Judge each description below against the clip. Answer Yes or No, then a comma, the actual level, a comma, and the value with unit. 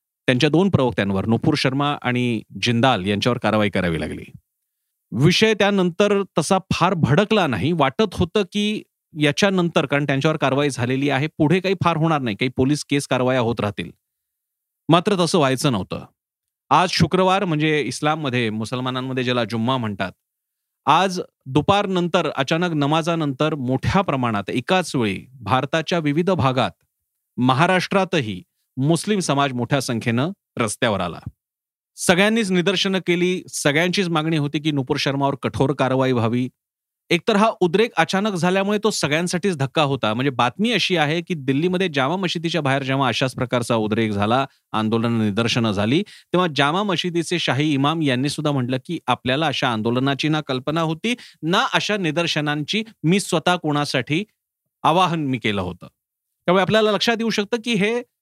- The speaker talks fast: Yes, fast, 140 wpm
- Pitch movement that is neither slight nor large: No, wide, 5.9 semitones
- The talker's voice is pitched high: No, medium, 150 Hz